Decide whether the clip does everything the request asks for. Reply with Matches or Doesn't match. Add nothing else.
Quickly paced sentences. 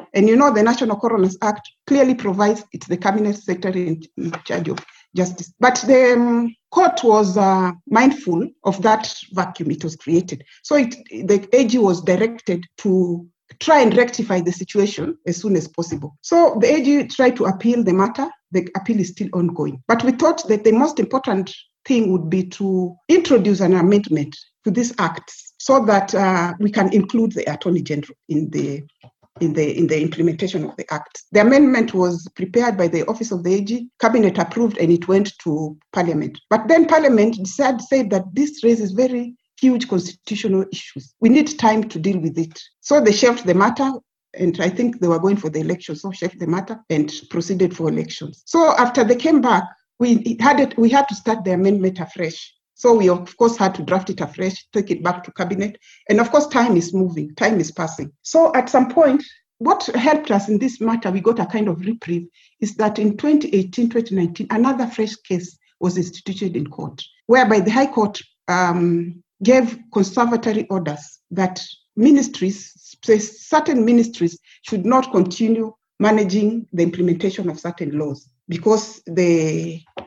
Doesn't match